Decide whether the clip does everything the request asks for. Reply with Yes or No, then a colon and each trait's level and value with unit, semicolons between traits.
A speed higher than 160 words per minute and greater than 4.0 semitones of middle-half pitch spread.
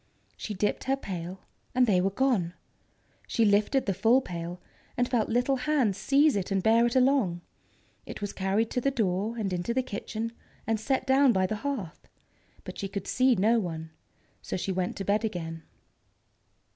Yes: average, 185 wpm; average, 5.0 semitones